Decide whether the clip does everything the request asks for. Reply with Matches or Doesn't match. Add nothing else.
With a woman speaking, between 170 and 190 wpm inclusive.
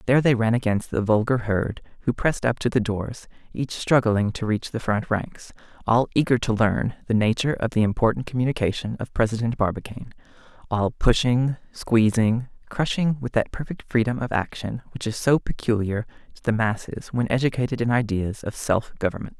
Doesn't match